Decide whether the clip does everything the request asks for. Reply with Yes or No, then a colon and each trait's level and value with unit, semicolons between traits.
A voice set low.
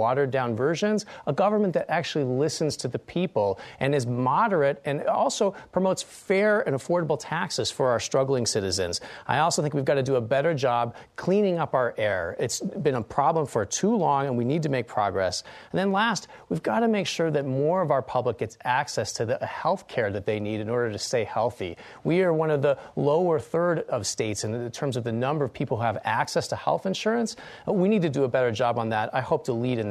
No: medium, 145 Hz